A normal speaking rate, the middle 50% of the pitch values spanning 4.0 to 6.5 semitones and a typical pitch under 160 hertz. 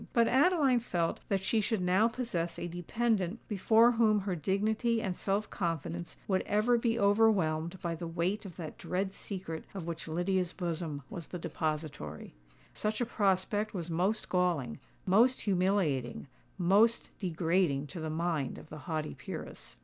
No: average, 150 wpm; average, 4.4 semitones; medium, 185 Hz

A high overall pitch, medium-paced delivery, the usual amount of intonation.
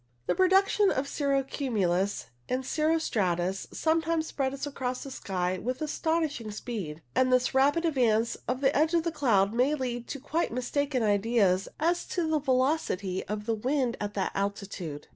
No: very high, 255 Hz; average, 165 wpm; wide, 6.5 semitones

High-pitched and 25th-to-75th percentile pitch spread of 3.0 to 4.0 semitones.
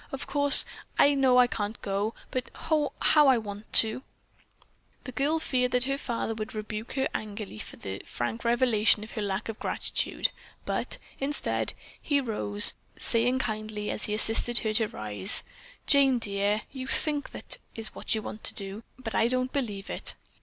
Yes: high, 225 Hz; average, 3.7 semitones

